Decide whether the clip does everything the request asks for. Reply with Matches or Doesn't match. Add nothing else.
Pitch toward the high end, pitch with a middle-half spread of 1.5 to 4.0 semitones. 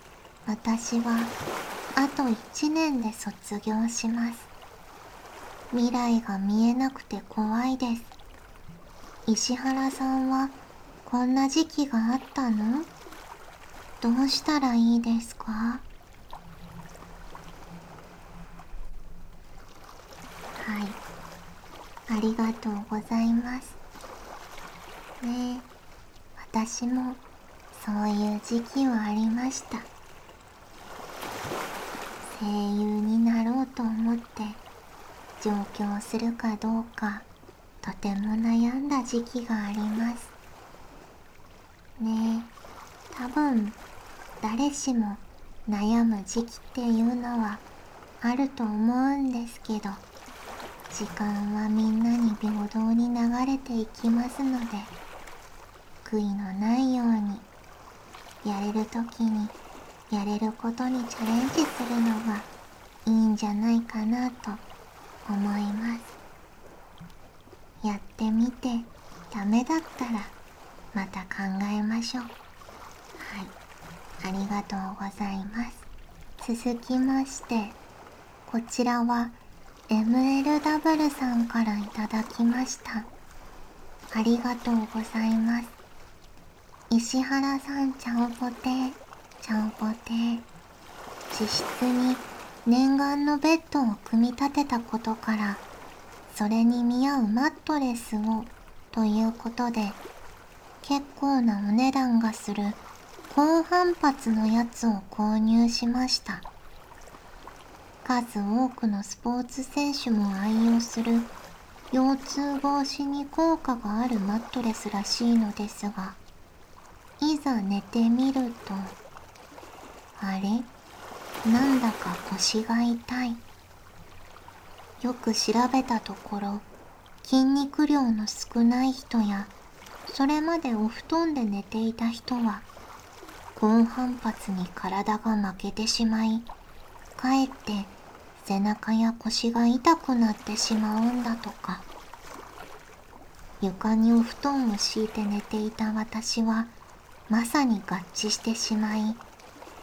Matches